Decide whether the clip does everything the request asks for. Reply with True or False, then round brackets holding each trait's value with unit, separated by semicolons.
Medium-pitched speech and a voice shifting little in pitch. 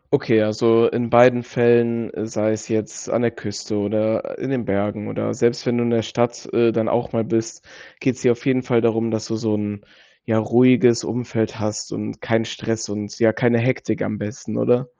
False (115 Hz; 1.7 semitones)